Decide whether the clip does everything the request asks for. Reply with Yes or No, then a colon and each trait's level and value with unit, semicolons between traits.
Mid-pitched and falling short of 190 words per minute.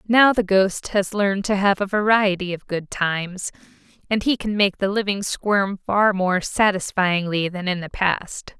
No: high, 195 Hz; average, 180 wpm